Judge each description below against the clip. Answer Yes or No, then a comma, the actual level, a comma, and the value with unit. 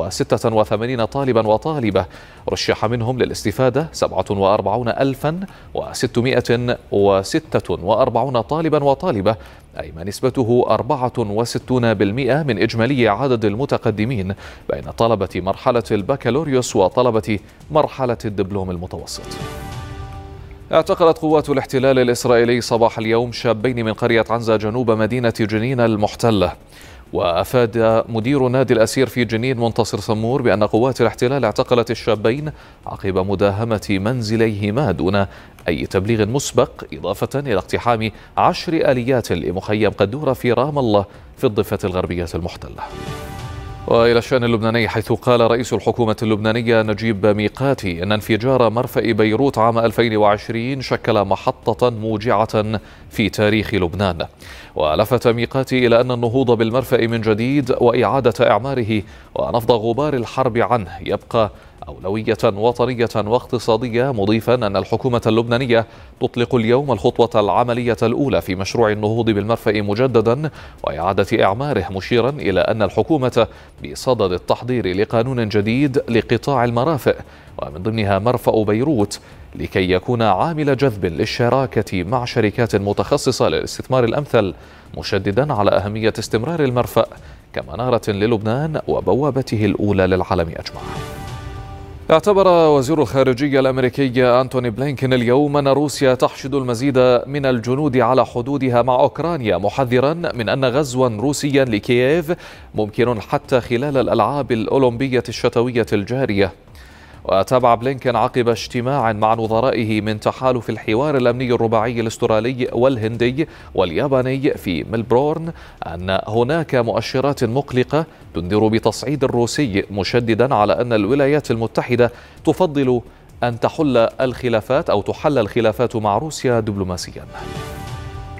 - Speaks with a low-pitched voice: Yes, low, 115 Hz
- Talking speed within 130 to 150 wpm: No, average, 110 wpm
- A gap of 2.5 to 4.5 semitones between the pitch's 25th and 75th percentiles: Yes, average, 3.4 semitones